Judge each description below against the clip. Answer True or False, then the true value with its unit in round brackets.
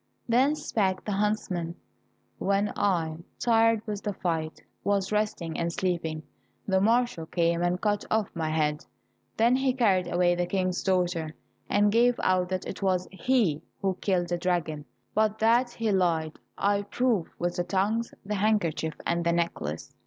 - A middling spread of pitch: True (3.8 semitones)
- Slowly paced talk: False (165 wpm)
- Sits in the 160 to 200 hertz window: True (190 Hz)